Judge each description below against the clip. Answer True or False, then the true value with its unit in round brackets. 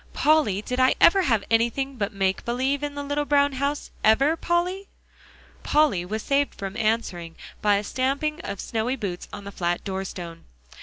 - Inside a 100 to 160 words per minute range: False (170 wpm)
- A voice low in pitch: False (250 Hz)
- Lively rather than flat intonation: True (6.2 semitones)